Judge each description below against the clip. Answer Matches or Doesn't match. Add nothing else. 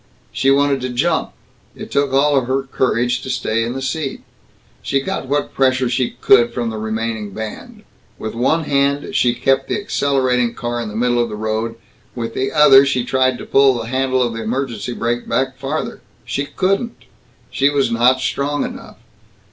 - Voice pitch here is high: Doesn't match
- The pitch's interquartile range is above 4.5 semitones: Doesn't match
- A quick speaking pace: Doesn't match